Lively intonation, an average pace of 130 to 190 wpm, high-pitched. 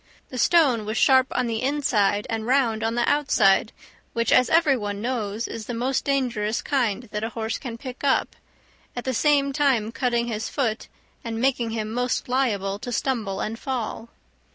No: average, 3.1 semitones; average, 180 wpm; high, 235 Hz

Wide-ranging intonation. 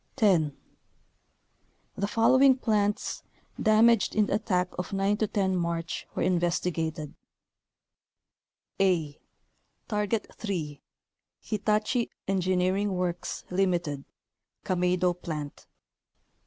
No: average, 3.2 semitones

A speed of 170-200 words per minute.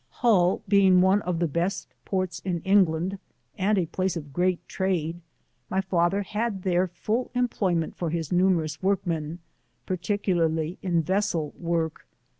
No: average, 145 wpm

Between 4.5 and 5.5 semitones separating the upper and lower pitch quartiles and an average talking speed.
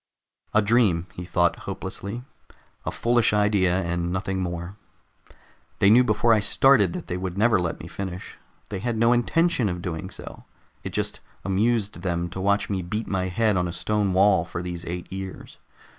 No: average, 3.5 semitones; average, 180 wpm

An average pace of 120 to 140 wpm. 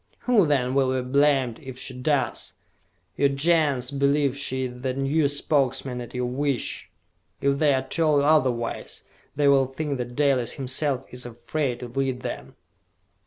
No: average, 160 wpm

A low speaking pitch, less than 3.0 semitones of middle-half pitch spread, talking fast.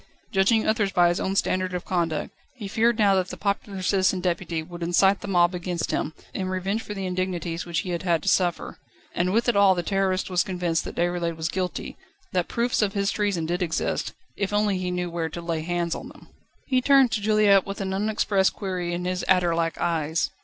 No: medium, 185 Hz; narrow, 2.4 semitones; fast, 220 wpm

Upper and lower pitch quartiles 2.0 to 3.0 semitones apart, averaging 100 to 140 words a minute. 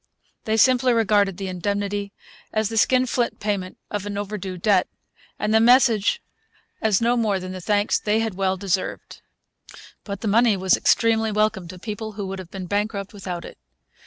No: narrow, 2.5 semitones; average, 175 wpm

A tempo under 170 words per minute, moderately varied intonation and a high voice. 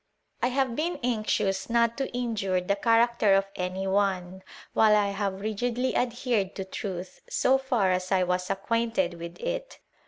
Yes: average, 155 wpm; average, 4.1 semitones; high, 210 Hz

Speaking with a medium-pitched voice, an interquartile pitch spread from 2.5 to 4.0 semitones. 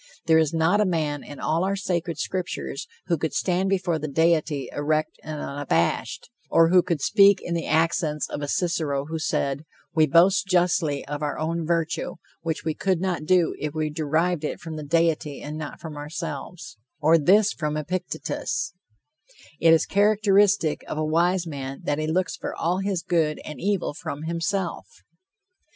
Yes: medium, 165 Hz; average, 2.8 semitones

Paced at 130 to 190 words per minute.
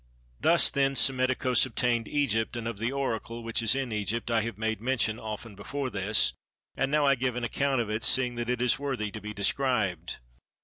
No: fast, 205 wpm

